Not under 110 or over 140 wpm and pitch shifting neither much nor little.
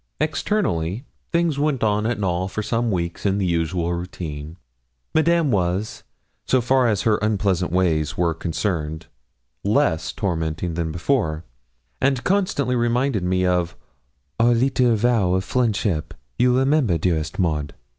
No: slow, 135 wpm; wide, 6.3 semitones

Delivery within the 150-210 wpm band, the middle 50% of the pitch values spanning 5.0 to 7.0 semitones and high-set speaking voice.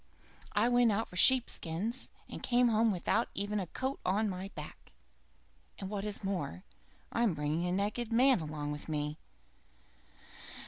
Yes: average, 155 wpm; average, 5.3 semitones; high, 200 Hz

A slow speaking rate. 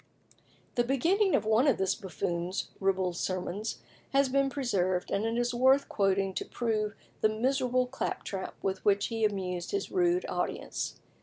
No: average, 150 wpm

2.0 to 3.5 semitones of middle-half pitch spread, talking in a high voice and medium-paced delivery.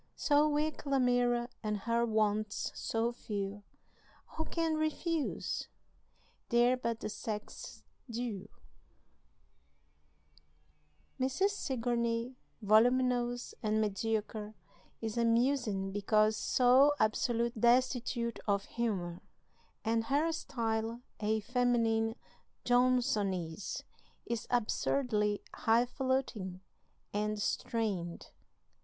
No: average, 2.8 semitones; high, 230 Hz; slow, 85 wpm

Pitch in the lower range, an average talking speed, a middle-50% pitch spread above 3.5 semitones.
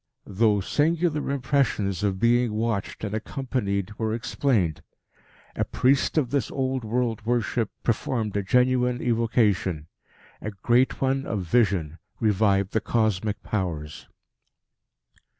No: low, 110 Hz; slow, 115 wpm; average, 3.9 semitones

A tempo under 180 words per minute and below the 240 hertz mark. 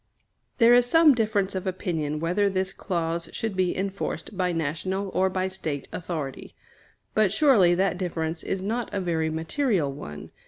Yes: average, 160 wpm; medium, 185 Hz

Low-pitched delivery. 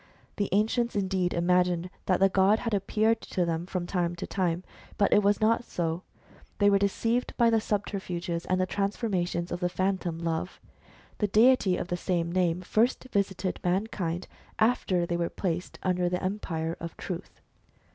No: medium, 185 Hz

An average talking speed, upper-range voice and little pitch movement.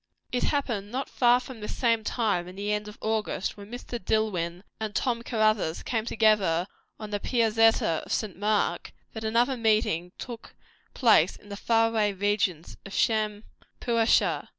Yes: average, 160 wpm; high, 215 Hz; narrow, 2.2 semitones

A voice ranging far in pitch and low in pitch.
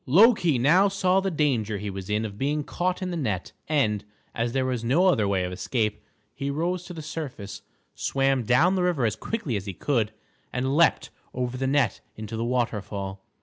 Yes: wide, 7.1 semitones; low, 130 Hz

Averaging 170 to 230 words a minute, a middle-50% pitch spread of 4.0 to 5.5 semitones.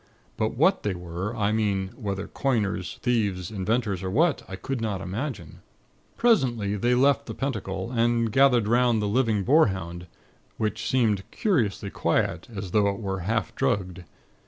No: average, 155 wpm; average, 4.3 semitones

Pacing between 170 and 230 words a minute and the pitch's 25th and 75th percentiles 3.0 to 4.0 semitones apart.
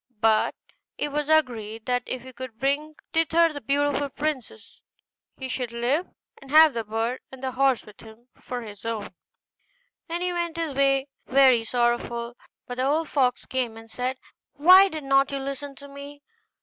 Yes: average, 175 wpm; average, 3.4 semitones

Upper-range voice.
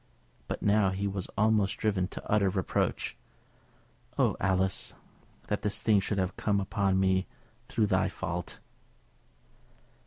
No: low, 100 Hz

